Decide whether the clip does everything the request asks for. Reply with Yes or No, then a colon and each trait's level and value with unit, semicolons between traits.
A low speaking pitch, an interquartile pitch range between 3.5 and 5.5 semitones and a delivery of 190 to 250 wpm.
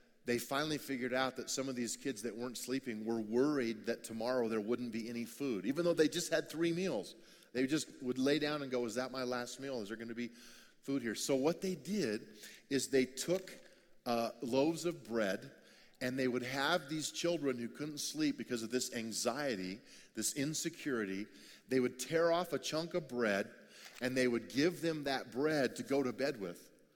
Yes: low, 130 Hz; average, 4.2 semitones; fast, 205 wpm